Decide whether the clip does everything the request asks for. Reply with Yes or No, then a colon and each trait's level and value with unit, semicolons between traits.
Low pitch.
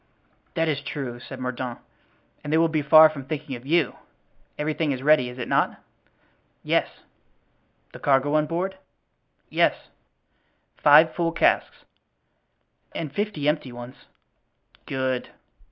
No: medium, 145 Hz